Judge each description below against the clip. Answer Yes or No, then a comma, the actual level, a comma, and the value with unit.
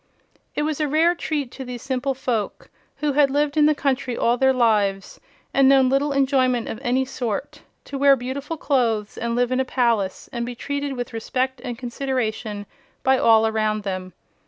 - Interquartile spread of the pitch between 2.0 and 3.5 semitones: Yes, average, 3.0 semitones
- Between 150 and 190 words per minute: Yes, average, 185 wpm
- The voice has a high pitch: Yes, very high, 255 Hz